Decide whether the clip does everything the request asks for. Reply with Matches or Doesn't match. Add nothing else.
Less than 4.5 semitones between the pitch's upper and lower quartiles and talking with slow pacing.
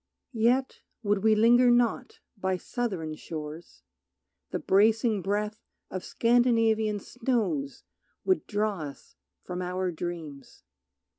Doesn't match